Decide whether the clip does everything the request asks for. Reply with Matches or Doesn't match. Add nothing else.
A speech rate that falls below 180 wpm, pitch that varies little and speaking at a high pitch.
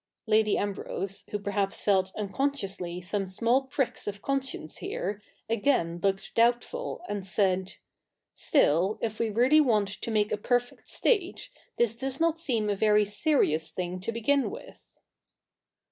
Doesn't match